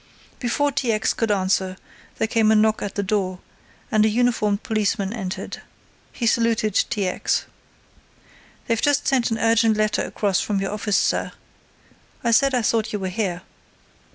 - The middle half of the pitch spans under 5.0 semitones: Yes, narrow, 2.4 semitones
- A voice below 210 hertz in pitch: No, high, 215 Hz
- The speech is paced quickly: No, average, 165 wpm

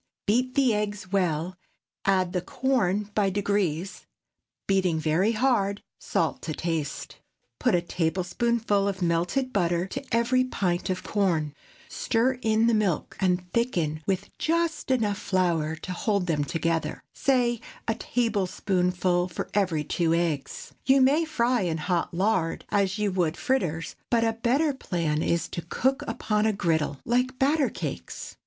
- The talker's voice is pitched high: Yes, high, 195 Hz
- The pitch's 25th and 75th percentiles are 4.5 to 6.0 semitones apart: Yes, average, 5.2 semitones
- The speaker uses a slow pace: No, average, 145 wpm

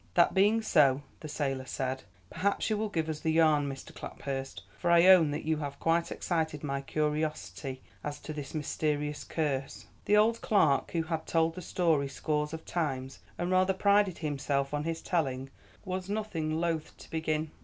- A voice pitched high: No, medium, 155 Hz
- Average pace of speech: Yes, average, 180 wpm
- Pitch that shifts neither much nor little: Yes, average, 3.3 semitones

